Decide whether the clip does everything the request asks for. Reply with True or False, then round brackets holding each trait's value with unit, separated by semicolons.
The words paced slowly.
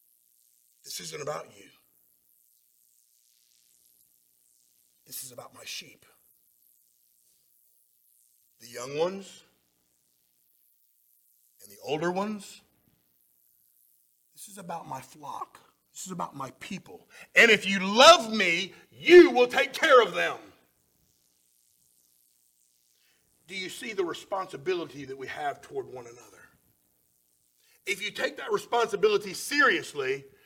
True (105 wpm)